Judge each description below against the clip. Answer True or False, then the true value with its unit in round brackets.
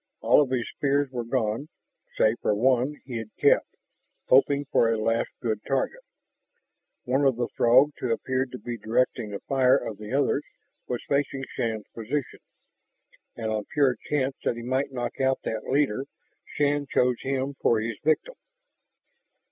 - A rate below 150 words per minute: False (165 wpm)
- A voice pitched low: True (130 Hz)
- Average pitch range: True (3.1 semitones)